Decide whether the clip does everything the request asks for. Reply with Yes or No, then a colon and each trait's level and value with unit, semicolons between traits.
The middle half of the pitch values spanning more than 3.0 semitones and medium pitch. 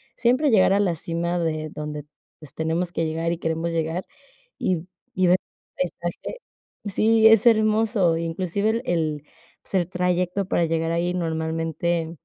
No: average, 2.7 semitones; medium, 170 Hz